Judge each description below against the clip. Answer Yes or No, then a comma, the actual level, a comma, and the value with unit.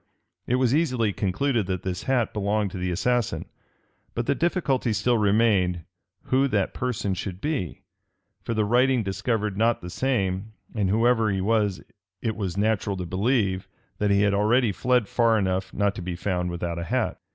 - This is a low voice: Yes, low, 105 Hz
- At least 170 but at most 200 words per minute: Yes, average, 175 wpm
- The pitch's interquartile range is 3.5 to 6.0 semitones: Yes, average, 4.1 semitones